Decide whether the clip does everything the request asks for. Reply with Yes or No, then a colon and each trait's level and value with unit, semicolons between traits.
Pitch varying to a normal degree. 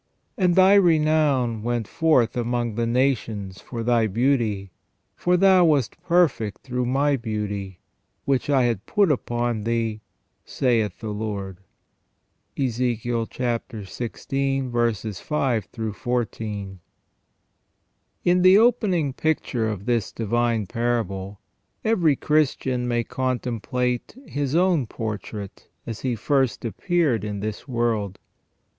Yes: average, 4.1 semitones